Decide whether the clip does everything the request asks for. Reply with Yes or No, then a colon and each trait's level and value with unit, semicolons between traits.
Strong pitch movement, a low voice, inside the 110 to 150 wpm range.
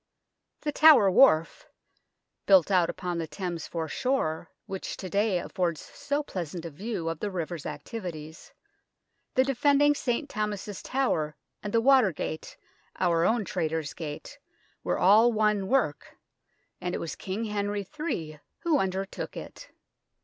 No: wide, 5.7 semitones; high, 190 Hz; average, 140 wpm